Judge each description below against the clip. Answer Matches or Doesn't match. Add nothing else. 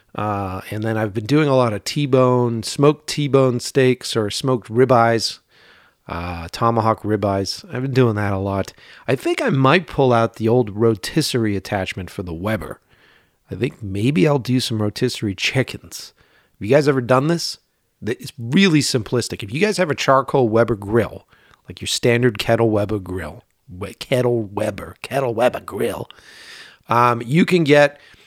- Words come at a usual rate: Matches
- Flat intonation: Doesn't match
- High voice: Doesn't match